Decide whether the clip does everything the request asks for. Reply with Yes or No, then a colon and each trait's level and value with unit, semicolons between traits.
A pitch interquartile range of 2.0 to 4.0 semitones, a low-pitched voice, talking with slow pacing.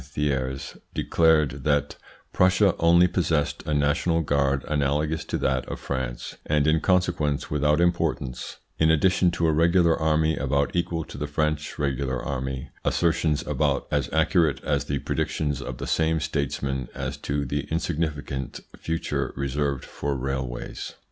No: average, 2.8 semitones; very low, 75 Hz; average, 145 wpm